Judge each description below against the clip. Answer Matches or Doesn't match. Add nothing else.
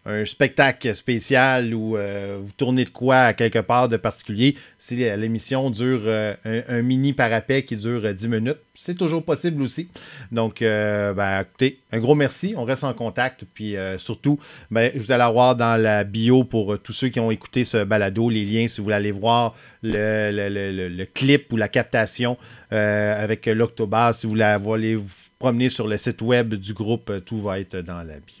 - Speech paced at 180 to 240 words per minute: Matches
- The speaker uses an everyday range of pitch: Matches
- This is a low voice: Matches